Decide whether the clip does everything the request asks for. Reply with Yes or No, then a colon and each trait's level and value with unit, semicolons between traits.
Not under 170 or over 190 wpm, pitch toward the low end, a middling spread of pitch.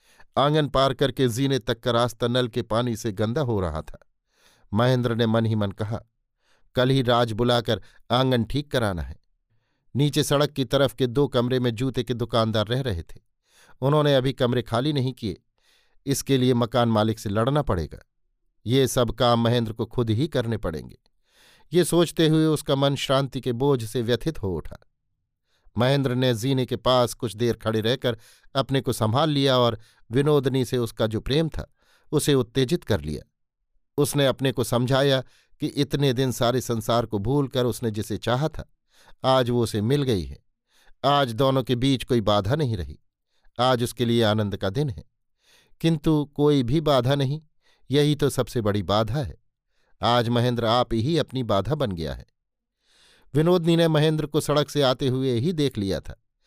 Yes: average, 180 wpm; low, 125 Hz; average, 3.4 semitones